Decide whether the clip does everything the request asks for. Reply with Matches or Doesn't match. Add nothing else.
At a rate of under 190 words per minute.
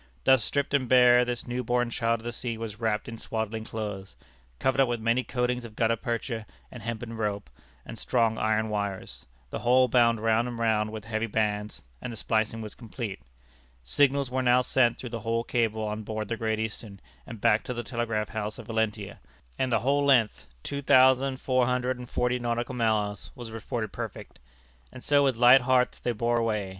Doesn't match